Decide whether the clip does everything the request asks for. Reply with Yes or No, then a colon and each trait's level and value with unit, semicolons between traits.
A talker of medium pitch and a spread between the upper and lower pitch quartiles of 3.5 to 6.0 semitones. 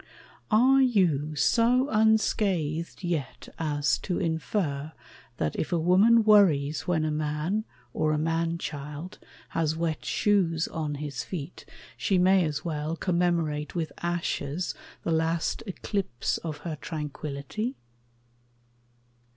Yes: medium, 165 Hz; average, 3.8 semitones